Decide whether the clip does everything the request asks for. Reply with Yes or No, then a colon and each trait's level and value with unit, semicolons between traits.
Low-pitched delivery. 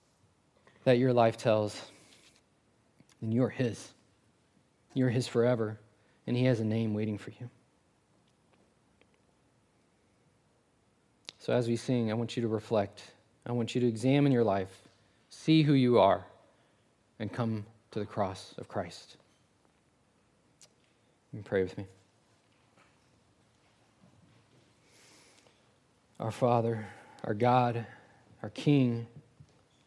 Yes: low, 115 Hz